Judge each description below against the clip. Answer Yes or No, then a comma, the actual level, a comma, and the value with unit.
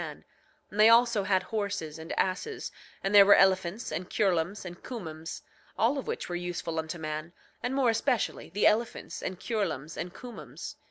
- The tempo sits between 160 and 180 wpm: Yes, average, 175 wpm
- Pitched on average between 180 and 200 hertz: Yes, high, 190 Hz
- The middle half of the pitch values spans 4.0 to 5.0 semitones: Yes, average, 4.6 semitones